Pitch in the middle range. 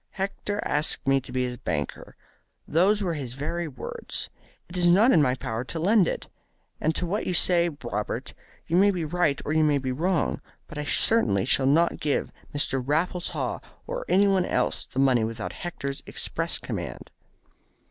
Yes: medium, 155 Hz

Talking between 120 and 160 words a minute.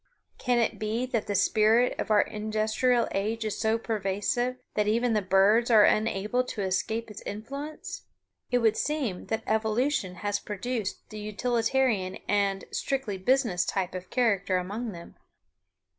Yes: average, 150 wpm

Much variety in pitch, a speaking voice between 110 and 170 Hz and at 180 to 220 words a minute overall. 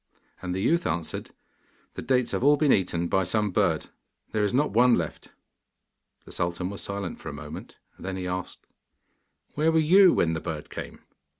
No: wide, 7.0 semitones; very low, 95 Hz; average, 185 wpm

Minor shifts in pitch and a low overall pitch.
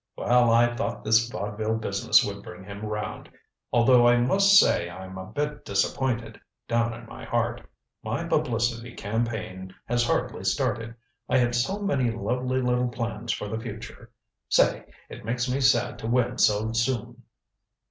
Yes: narrow, 2.0 semitones; low, 115 Hz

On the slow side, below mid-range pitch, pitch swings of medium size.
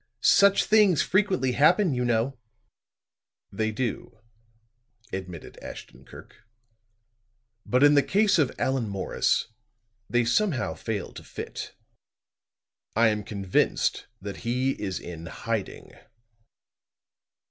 No: slow, 105 wpm; low, 120 Hz; wide, 6.2 semitones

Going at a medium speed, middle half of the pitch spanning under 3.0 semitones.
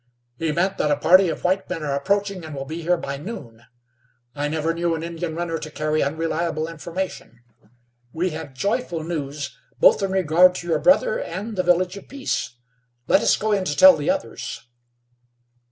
No: average, 185 wpm; average, 3.6 semitones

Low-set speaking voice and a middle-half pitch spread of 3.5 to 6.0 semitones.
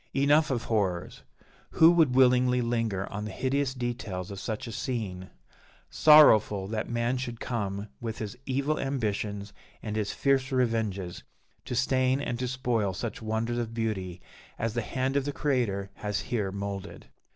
Yes: low, 115 Hz; average, 4.0 semitones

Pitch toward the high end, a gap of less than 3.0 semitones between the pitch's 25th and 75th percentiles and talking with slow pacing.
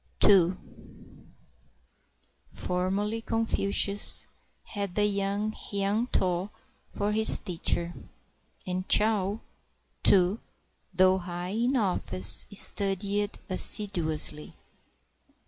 Yes: high, 200 Hz; narrow, 2.4 semitones; slow, 80 wpm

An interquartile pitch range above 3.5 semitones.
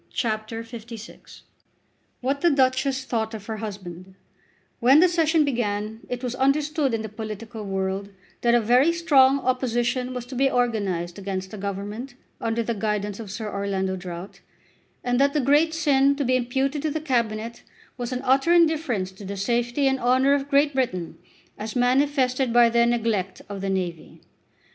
Yes: average, 4.5 semitones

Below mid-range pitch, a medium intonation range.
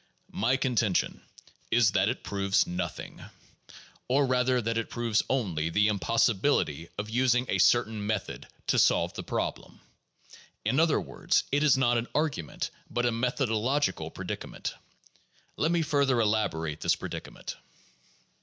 Yes: low, 115 Hz; average, 4.0 semitones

